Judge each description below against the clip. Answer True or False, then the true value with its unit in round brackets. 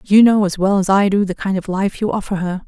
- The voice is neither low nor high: False (195 Hz)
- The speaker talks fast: True (315 wpm)